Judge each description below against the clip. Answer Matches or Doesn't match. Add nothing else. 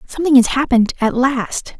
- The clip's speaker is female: Matches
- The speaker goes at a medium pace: Matches